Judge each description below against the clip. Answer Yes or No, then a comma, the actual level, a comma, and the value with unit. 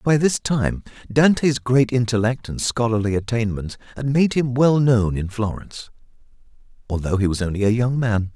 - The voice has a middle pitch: No, low, 115 Hz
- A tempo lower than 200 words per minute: Yes, average, 165 wpm